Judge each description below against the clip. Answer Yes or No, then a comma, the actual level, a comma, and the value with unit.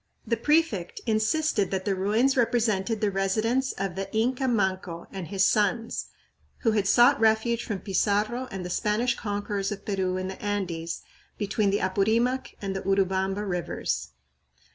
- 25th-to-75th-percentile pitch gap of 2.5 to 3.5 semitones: Yes, average, 3.1 semitones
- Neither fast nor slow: Yes, average, 150 wpm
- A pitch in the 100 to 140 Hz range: No, high, 205 Hz